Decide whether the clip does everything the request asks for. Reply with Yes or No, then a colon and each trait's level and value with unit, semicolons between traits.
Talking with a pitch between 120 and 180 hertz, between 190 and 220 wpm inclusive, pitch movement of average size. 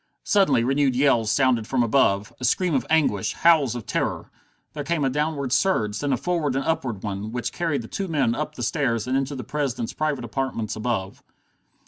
Yes: low, 135 Hz; average, 195 wpm; average, 4.3 semitones